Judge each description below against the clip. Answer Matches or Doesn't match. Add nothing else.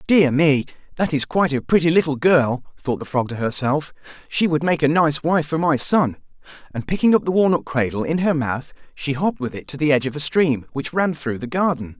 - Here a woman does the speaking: Doesn't match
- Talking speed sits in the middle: Doesn't match